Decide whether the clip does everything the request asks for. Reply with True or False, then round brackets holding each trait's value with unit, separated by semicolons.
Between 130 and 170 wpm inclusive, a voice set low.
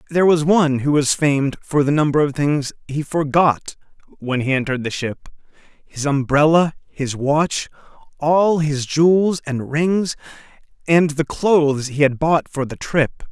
False (160 wpm; 150 Hz)